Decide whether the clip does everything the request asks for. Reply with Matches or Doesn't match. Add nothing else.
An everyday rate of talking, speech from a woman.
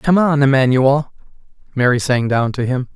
Doesn't match